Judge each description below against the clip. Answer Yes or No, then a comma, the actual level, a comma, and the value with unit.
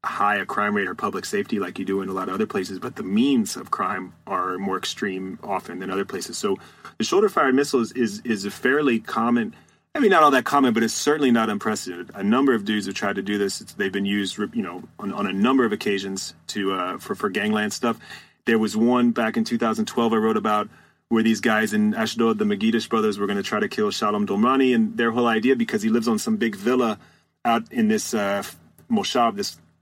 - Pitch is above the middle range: No, low, 110 Hz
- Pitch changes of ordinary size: Yes, average, 3.4 semitones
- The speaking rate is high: Yes, fast, 235 wpm